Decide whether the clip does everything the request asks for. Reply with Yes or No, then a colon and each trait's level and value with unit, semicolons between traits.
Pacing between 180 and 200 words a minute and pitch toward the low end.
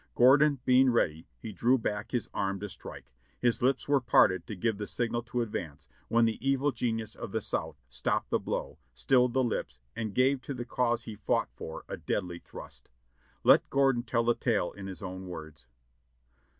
Yes: average, 190 wpm; low, 115 Hz